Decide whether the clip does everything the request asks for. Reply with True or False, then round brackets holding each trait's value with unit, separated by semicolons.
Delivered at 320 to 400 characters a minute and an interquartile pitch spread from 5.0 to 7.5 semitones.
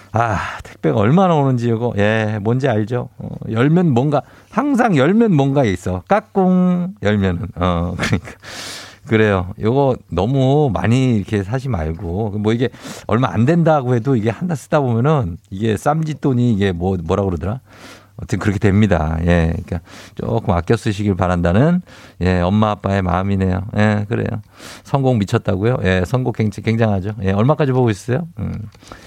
True (330 characters per minute; 5.3 semitones)